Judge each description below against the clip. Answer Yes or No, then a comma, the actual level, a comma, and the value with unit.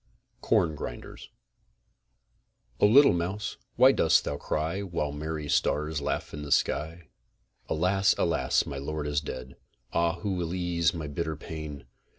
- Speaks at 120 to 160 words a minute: Yes, average, 145 wpm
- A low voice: Yes, very low, 80 Hz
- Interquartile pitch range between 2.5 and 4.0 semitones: Yes, average, 2.8 semitones